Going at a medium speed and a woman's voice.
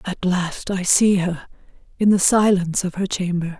Yes: average, 185 wpm; female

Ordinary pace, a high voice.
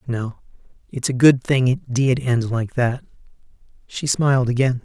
No: average, 160 wpm; low, 125 Hz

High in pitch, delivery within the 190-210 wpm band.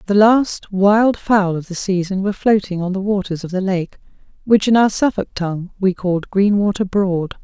Yes: high, 195 Hz; average, 195 wpm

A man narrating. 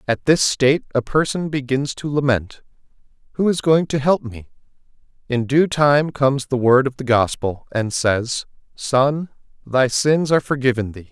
Yes: male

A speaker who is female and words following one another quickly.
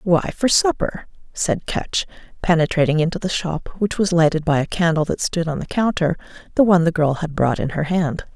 Yes: female; fast, 210 wpm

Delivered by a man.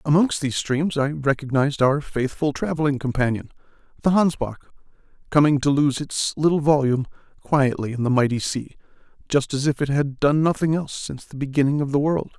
Yes: male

